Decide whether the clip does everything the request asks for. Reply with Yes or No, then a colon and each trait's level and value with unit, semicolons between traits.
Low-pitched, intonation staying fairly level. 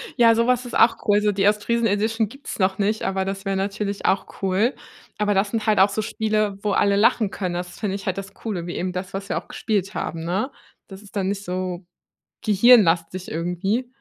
No: high, 200 Hz; narrow, 2.3 semitones